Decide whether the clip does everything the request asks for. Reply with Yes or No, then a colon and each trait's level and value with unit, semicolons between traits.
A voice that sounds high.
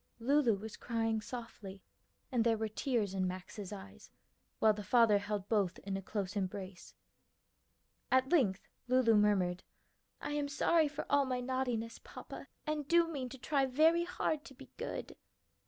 Yes: high, 230 Hz